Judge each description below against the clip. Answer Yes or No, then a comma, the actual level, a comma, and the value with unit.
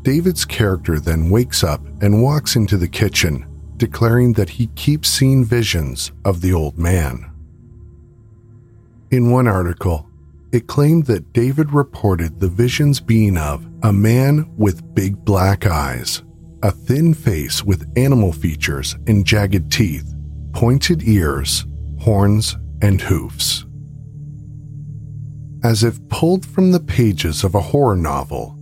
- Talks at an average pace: No, slow, 130 wpm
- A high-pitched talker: No, low, 105 Hz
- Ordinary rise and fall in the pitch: No, wide, 7.5 semitones